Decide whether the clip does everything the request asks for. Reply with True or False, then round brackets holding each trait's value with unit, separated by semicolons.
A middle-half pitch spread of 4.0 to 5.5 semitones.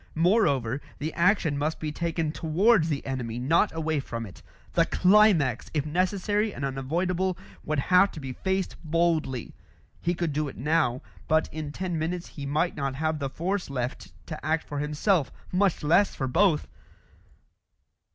True (4.3 semitones)